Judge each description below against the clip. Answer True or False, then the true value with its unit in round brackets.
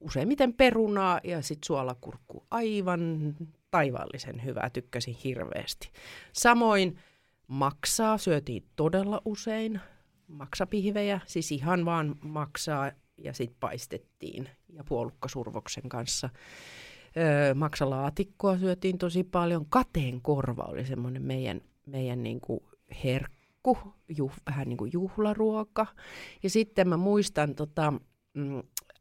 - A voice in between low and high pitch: True (155 Hz)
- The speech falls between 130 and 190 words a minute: False (105 wpm)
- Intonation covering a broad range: True (6.5 semitones)